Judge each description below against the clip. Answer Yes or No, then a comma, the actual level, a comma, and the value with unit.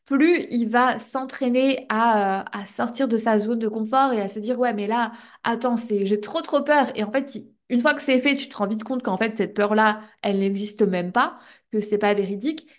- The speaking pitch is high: Yes, high, 230 Hz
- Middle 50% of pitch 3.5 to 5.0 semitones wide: Yes, average, 4.0 semitones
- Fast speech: Yes, fast, 240 wpm